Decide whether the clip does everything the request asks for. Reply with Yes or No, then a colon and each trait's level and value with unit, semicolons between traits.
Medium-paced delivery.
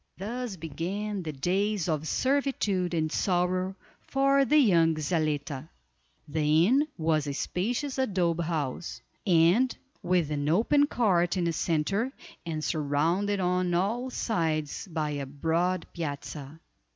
No: slow, 125 wpm